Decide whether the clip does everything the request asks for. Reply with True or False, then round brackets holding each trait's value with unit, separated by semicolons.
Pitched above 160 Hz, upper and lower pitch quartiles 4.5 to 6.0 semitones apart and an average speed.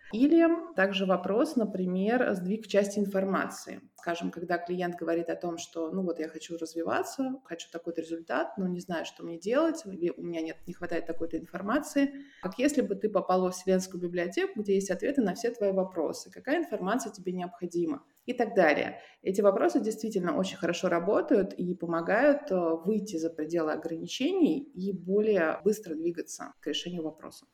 False (190 Hz; 5.5 semitones; 165 wpm)